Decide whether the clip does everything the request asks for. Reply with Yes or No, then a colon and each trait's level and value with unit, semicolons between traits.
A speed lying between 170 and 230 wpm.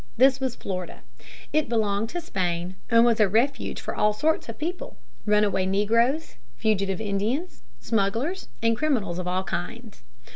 No: average, 150 wpm